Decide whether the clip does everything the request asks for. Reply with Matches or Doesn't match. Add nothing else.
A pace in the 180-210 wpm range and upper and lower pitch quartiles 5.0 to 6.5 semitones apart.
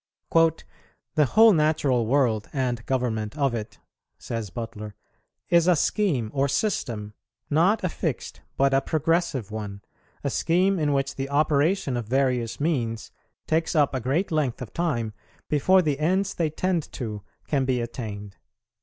Doesn't match